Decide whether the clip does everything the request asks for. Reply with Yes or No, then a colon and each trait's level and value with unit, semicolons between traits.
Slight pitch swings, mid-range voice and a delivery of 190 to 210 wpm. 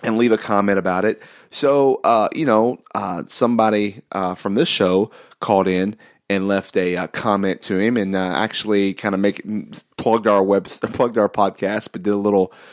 No: narrow, 2.1 semitones; low, 100 Hz; average, 200 wpm